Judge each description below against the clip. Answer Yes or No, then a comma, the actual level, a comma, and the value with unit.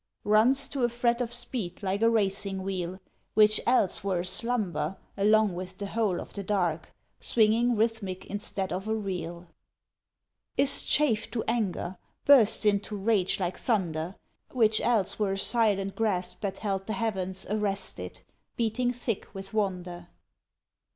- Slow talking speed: No, average, 145 wpm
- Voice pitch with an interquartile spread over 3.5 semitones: No, average, 3.1 semitones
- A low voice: No, high, 205 Hz